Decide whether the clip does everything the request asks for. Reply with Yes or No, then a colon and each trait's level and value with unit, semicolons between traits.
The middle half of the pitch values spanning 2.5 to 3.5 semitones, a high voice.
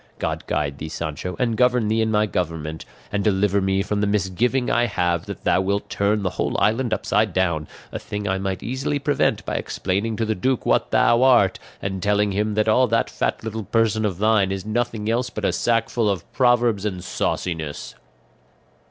No: average, 3.1 semitones; low, 105 Hz